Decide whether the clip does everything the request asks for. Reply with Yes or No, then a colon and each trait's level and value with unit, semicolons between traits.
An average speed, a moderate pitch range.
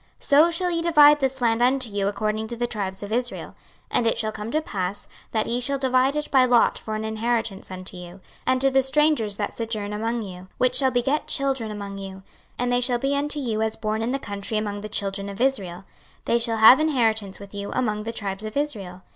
No: fast, 235 wpm; average, 4.3 semitones